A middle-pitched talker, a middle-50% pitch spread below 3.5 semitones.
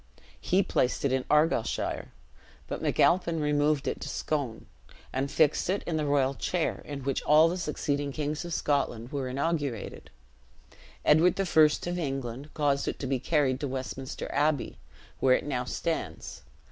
Yes: medium, 145 Hz; average, 2.8 semitones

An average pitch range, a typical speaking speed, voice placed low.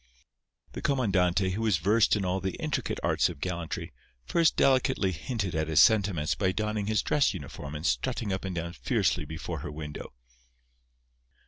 Yes: average, 4.6 semitones; average, 165 wpm; very low, 95 Hz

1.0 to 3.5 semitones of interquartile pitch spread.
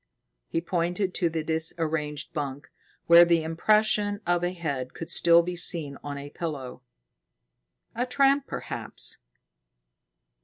Yes: average, 2.9 semitones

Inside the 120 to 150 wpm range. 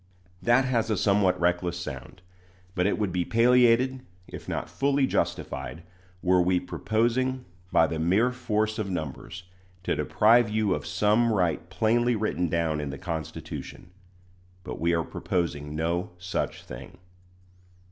Yes: average, 145 wpm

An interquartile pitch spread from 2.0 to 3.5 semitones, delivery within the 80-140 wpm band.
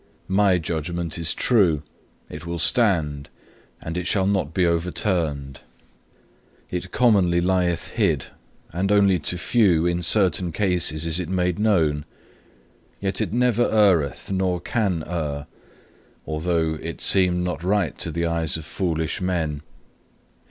Yes: average, 2.8 semitones; slow, 135 wpm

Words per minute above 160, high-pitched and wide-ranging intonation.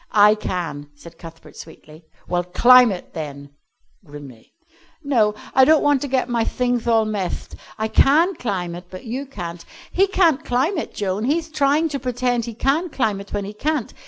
Yes: average, 185 wpm; high, 230 Hz; wide, 7.4 semitones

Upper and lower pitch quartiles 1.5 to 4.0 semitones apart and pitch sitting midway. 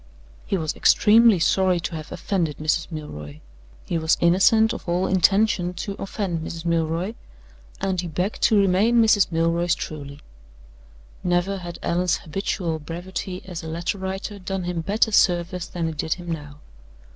Yes: average, 2.8 semitones; medium, 175 Hz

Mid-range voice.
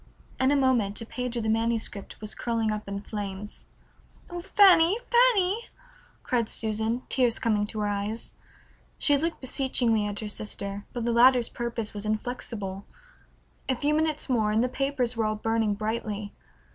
No: high, 230 Hz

